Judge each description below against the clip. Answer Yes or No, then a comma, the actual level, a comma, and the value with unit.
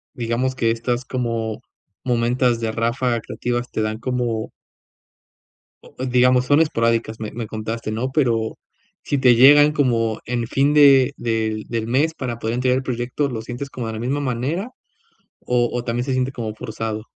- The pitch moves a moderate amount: No, narrow, 2.2 semitones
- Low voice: Yes, low, 120 Hz